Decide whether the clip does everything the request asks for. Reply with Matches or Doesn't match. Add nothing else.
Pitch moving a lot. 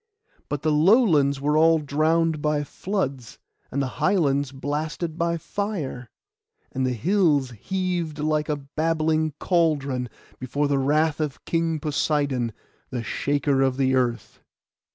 Doesn't match